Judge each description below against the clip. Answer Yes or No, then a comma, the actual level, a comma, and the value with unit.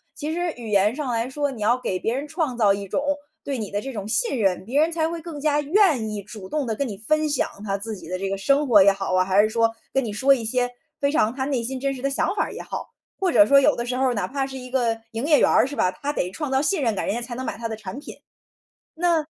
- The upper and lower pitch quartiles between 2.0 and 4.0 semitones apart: No, average, 5.2 semitones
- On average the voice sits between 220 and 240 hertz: No, very high, 250 Hz